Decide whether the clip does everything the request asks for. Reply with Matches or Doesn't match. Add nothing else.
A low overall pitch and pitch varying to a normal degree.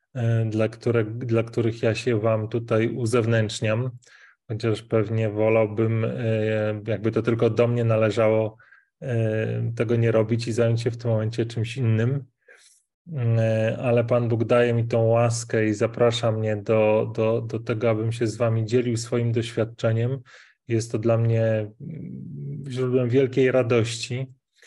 Doesn't match